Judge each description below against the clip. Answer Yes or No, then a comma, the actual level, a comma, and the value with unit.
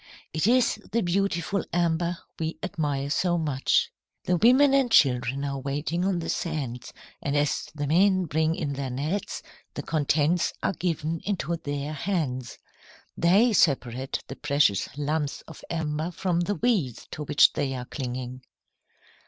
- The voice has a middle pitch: Yes, medium, 155 Hz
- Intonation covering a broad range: No, average, 4.1 semitones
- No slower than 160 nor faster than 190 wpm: No, average, 150 wpm